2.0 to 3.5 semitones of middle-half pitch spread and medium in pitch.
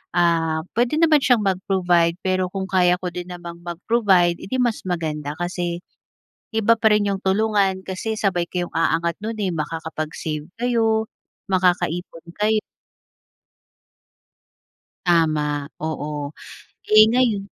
No: average, 4.0 semitones; medium, 180 Hz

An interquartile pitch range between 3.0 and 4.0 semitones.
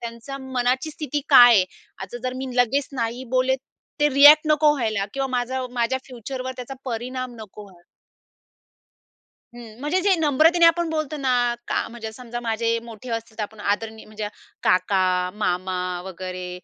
Yes: average, 3.7 semitones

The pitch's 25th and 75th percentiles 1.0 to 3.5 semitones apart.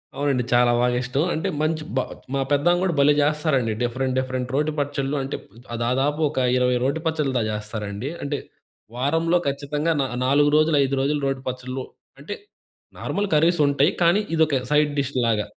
Yes: average, 2.9 semitones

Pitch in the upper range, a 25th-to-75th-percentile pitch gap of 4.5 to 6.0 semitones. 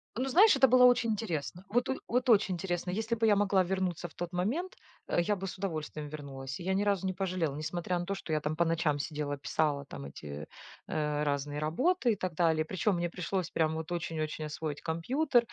No: medium, 175 Hz; average, 4.9 semitones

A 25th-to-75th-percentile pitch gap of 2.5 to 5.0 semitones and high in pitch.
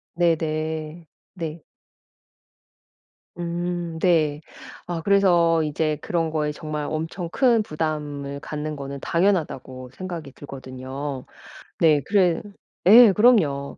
No: average, 2.8 semitones; medium, 160 Hz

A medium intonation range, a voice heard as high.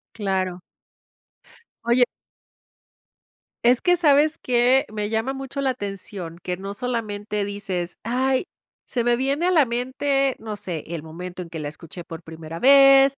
No: wide, 6.6 semitones; high, 225 Hz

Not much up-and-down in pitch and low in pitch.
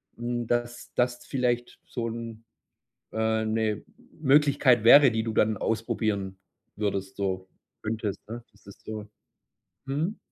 Yes: narrow, 2.1 semitones; low, 115 Hz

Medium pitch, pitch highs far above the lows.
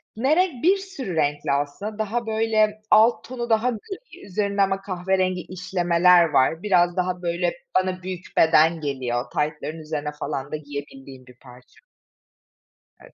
Yes: medium, 180 Hz; wide, 6.1 semitones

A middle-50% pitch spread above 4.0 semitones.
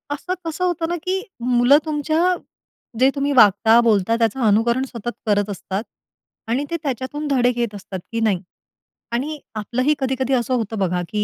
Yes: average, 5.0 semitones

